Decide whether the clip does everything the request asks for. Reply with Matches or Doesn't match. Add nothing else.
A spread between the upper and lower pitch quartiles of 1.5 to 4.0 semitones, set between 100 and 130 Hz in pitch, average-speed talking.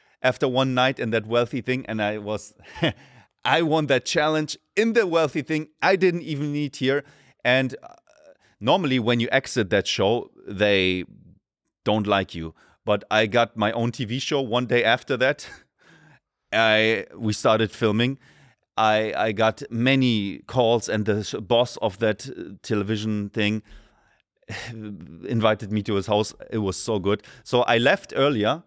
Matches